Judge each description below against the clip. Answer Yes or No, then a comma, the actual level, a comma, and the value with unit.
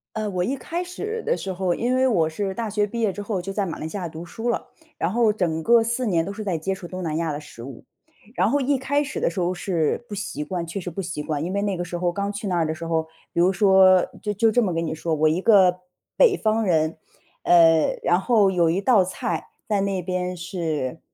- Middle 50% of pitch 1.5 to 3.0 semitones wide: No, average, 4.3 semitones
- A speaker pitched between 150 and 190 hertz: Yes, medium, 185 Hz